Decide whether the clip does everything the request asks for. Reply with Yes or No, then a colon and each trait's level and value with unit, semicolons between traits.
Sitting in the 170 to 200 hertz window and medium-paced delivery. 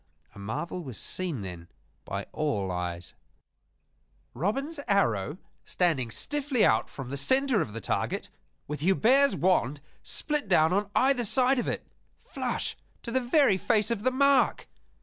Yes: medium, 185 Hz; average, 150 wpm